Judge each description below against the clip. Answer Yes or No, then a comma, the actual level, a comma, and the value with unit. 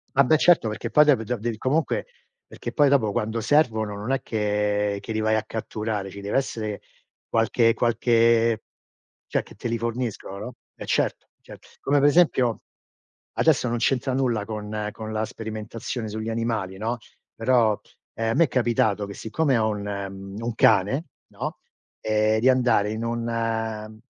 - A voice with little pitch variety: Yes, narrow, 2.1 semitones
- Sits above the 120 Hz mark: No, low, 115 Hz